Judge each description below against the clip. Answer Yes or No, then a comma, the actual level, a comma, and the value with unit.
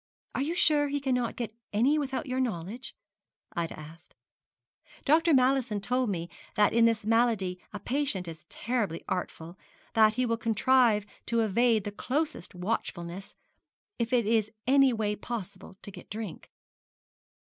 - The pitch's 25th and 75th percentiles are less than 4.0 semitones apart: No, average, 4.5 semitones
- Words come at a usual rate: Yes, average, 150 wpm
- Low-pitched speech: No, high, 225 Hz